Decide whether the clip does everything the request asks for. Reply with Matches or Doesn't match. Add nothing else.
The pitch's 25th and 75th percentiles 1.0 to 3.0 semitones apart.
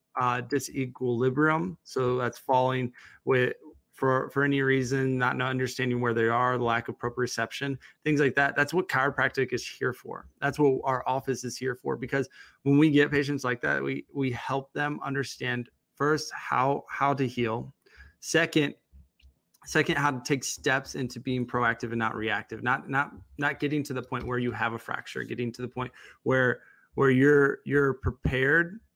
Matches